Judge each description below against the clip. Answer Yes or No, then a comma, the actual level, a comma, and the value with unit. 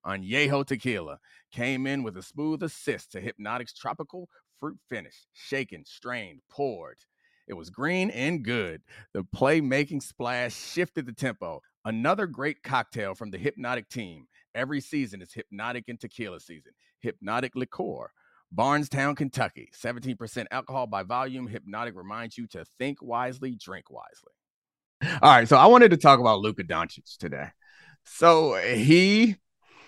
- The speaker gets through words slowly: No, average, 145 wpm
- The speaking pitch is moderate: No, low, 130 Hz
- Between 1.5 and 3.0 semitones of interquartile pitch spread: No, average, 3.8 semitones